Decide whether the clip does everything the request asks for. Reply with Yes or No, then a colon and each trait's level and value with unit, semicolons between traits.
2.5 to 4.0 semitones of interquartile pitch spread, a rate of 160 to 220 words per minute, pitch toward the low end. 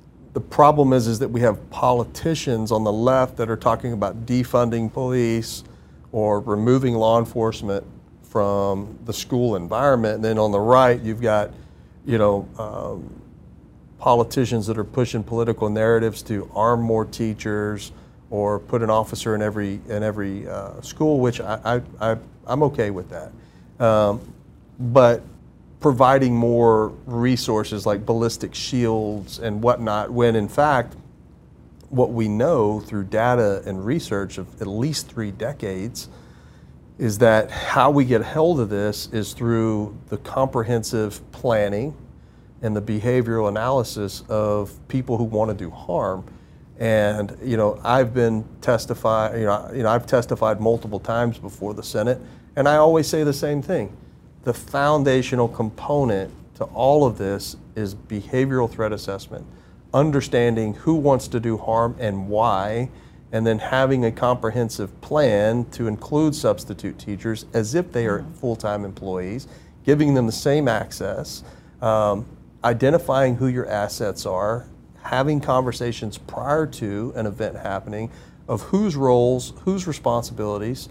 No: average, 3.1 semitones; average, 145 wpm; low, 115 Hz